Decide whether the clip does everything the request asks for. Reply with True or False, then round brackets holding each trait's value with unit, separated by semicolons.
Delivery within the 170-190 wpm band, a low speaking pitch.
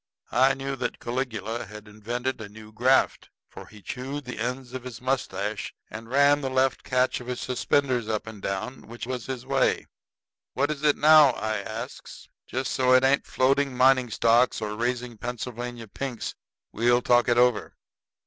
True (175 wpm; 125 Hz)